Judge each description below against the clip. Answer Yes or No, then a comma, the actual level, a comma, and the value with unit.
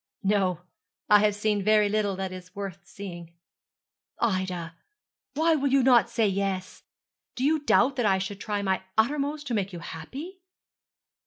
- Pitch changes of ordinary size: Yes, average, 4.9 semitones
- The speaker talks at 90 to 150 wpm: No, average, 160 wpm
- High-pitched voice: Yes, high, 205 Hz